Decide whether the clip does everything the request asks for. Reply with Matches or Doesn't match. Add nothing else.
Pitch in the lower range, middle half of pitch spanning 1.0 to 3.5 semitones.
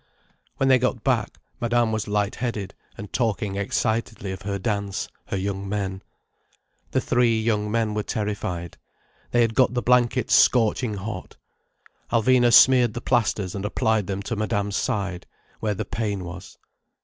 Matches